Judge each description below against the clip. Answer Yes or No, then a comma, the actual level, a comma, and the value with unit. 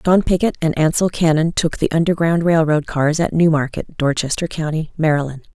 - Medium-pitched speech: Yes, medium, 160 Hz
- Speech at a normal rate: Yes, average, 185 wpm